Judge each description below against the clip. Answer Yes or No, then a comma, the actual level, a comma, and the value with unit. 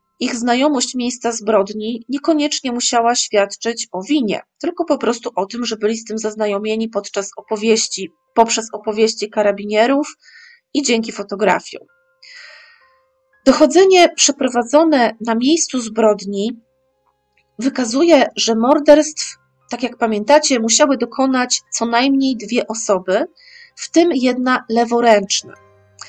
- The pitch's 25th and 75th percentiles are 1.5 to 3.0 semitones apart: No, average, 4.8 semitones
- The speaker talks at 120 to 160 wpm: No, slow, 110 wpm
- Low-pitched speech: No, high, 235 Hz